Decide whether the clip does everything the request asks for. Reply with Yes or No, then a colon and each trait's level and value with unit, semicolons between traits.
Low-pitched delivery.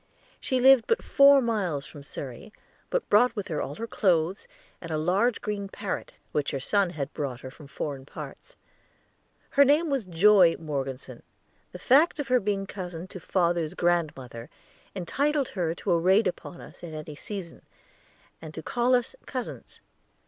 No: medium, 185 Hz